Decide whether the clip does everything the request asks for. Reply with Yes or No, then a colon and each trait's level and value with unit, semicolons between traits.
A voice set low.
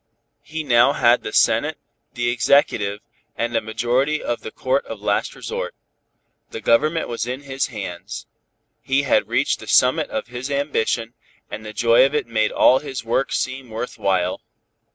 Yes: low, 120 Hz